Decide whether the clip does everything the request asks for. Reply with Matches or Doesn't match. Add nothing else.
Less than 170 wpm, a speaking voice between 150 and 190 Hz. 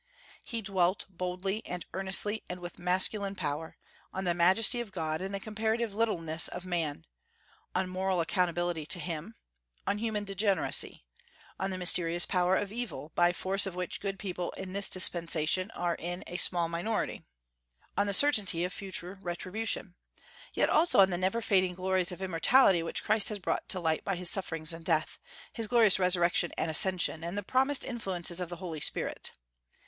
Doesn't match